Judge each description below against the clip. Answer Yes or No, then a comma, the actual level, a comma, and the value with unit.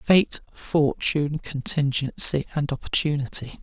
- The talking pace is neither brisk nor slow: No, slow, 85 wpm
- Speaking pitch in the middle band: Yes, medium, 145 Hz